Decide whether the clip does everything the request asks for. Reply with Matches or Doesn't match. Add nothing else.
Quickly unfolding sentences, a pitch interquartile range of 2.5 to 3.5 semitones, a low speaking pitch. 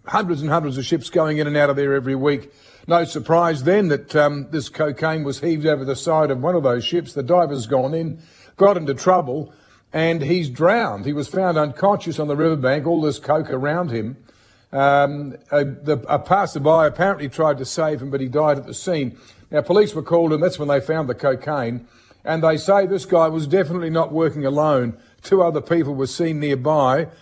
Doesn't match